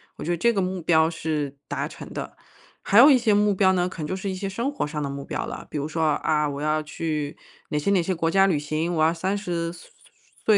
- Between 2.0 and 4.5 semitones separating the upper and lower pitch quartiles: Yes, average, 3.9 semitones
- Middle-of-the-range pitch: Yes, medium, 170 Hz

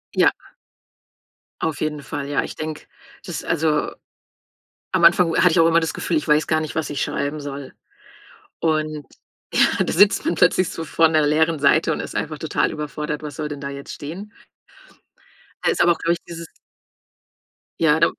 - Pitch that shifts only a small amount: Yes, narrow, 1.9 semitones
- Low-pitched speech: No, medium, 155 Hz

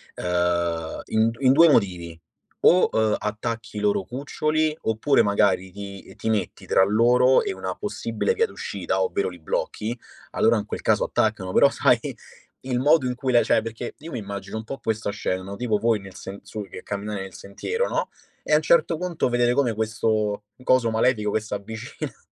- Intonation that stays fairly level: No, average, 4.4 semitones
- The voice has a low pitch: Yes, low, 110 Hz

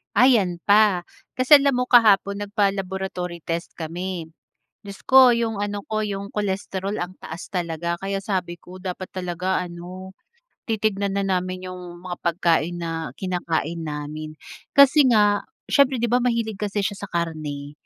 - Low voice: No, high, 190 Hz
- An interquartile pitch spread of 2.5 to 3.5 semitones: Yes, average, 3.1 semitones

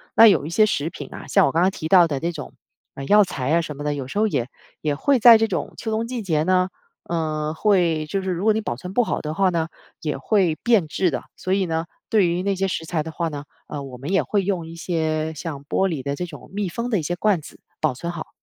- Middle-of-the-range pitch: Yes, medium, 170 Hz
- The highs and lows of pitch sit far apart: No, average, 4.2 semitones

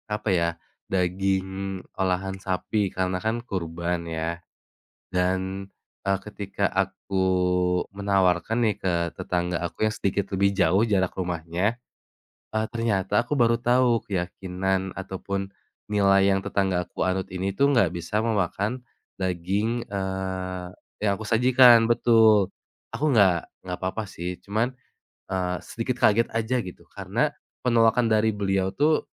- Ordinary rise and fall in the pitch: Yes, average, 3.0 semitones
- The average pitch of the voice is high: No, very low, 95 Hz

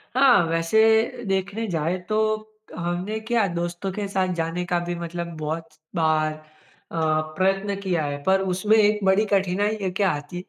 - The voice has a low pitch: No, high, 190 Hz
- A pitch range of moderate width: Yes, average, 3.5 semitones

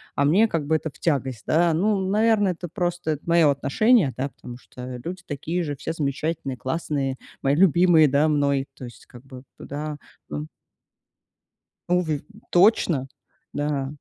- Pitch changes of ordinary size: Yes, average, 4.3 semitones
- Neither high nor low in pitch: Yes, medium, 150 Hz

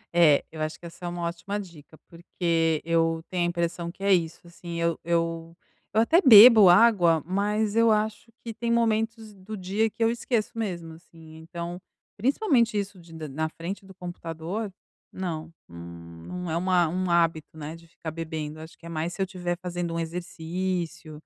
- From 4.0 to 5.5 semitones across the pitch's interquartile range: No, average, 3.6 semitones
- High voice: No, medium, 175 Hz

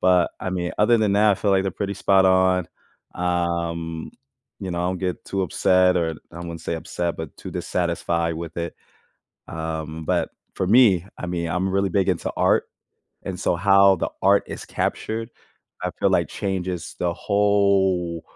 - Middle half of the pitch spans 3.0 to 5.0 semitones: No, narrow, 2.4 semitones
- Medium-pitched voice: No, very low, 90 Hz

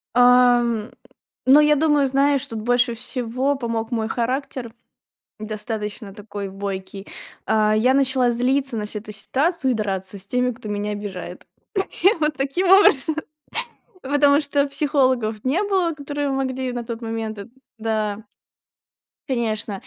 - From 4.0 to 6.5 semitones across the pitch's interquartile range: Yes, average, 4.3 semitones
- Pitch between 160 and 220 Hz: No, high, 245 Hz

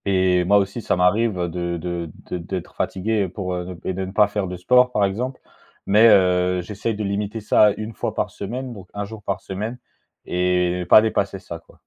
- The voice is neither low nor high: No, very low, 95 Hz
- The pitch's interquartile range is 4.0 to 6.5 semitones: No, average, 2.8 semitones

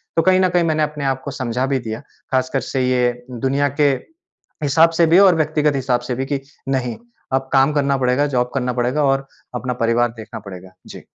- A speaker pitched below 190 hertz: Yes, low, 135 Hz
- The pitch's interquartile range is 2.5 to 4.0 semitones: Yes, average, 2.9 semitones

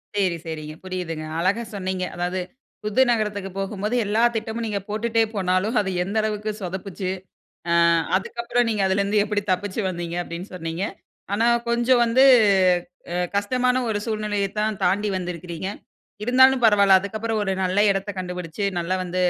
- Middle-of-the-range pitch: No, high, 200 Hz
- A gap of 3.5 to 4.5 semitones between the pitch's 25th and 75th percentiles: No, average, 3.0 semitones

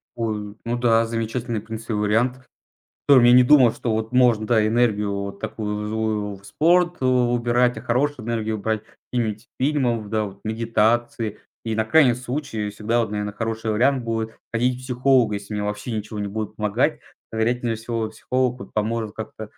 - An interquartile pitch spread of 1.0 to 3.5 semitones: Yes, narrow, 2.4 semitones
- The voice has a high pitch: No, low, 115 Hz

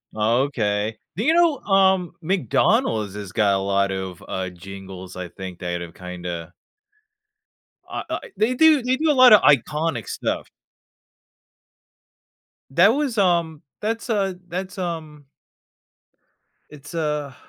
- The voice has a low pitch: No, medium, 150 Hz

